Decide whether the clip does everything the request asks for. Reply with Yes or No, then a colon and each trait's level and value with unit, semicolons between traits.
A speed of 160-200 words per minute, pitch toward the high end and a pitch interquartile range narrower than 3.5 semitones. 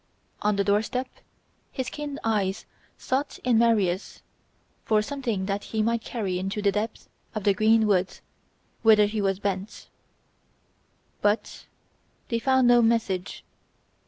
No: slow, 135 wpm; high, 215 Hz; average, 2.7 semitones